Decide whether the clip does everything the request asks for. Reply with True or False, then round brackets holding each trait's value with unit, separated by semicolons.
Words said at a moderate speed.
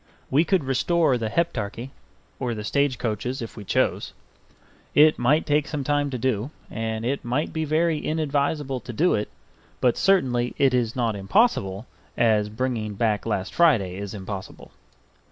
True (160 wpm)